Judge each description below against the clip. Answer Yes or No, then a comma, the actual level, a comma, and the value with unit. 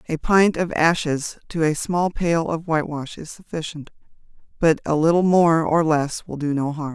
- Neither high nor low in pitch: Yes, medium, 160 Hz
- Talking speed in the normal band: Yes, average, 190 wpm